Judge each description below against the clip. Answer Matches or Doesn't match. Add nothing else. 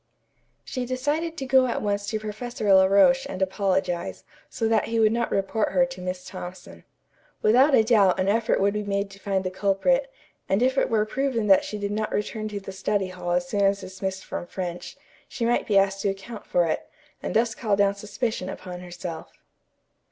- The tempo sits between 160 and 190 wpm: Doesn't match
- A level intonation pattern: Doesn't match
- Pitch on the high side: Matches